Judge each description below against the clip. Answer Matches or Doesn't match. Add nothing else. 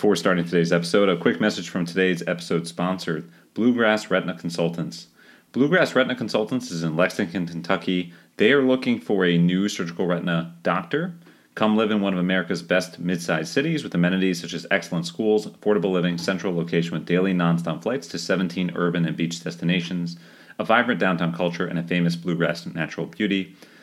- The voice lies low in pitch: Matches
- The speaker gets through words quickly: Doesn't match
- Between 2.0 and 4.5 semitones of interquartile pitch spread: Matches